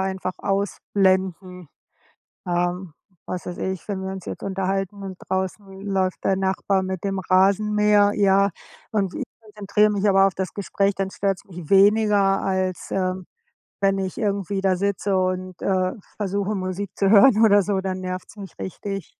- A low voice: No, high, 195 Hz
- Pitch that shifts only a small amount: Yes, narrow, 1.3 semitones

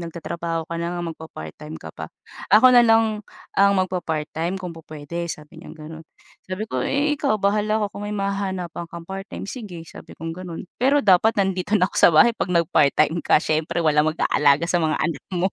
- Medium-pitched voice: Yes, medium, 170 Hz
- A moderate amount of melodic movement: Yes, average, 3.8 semitones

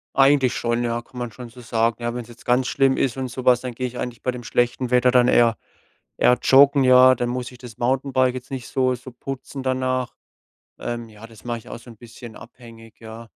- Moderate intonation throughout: No, narrow, 1.5 semitones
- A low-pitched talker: Yes, low, 125 Hz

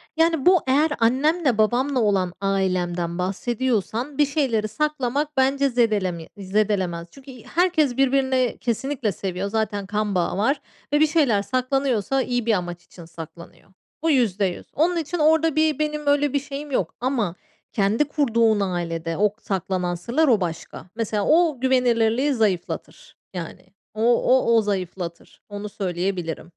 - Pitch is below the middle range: No, high, 230 Hz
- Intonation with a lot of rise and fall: Yes, wide, 6.3 semitones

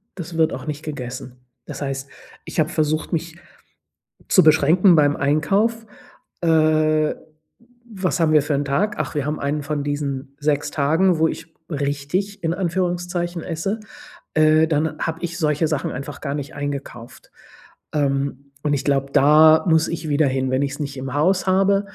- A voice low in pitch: No, medium, 155 Hz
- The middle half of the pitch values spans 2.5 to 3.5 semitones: Yes, average, 2.8 semitones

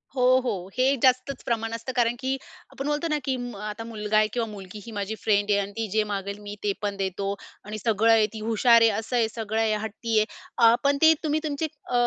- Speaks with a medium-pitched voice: No, high, 225 Hz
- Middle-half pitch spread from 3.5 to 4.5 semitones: No, average, 3.1 semitones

